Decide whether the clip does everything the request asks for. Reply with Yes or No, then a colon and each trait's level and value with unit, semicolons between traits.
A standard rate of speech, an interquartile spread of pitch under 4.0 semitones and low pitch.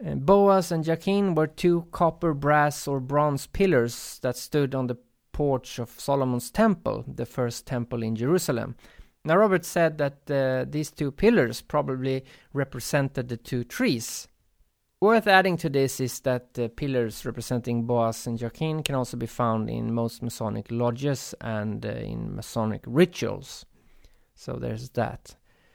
No: average, 150 wpm; average, 4.7 semitones; low, 130 Hz